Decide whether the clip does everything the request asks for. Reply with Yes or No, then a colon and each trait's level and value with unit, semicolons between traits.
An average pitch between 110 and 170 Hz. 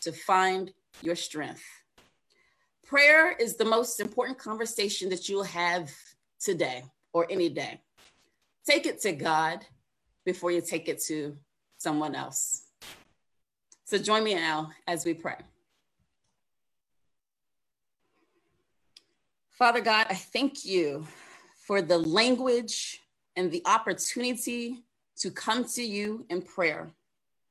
No: high, 195 Hz